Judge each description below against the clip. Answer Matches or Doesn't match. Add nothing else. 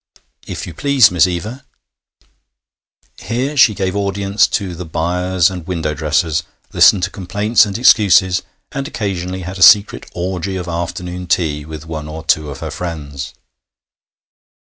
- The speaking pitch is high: Doesn't match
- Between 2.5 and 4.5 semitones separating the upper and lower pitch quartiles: Matches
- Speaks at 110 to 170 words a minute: Matches